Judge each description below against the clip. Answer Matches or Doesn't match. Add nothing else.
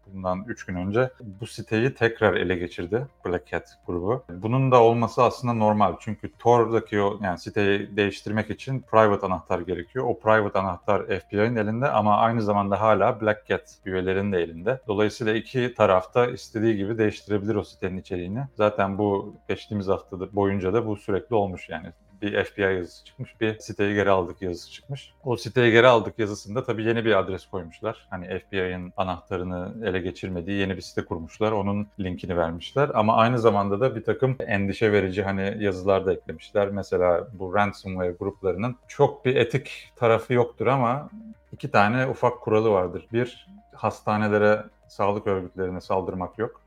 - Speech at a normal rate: Doesn't match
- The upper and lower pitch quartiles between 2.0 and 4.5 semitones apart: Matches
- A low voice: Matches